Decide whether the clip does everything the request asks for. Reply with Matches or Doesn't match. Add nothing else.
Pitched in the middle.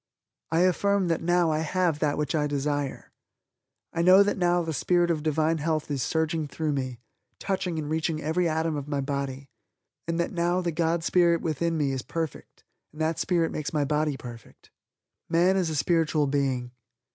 Matches